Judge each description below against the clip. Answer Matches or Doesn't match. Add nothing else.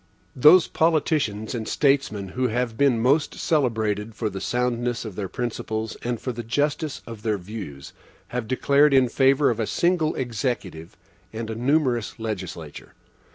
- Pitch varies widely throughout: Doesn't match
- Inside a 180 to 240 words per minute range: Doesn't match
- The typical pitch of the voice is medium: Doesn't match